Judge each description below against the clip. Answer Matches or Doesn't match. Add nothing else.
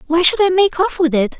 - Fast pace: Matches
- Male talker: Doesn't match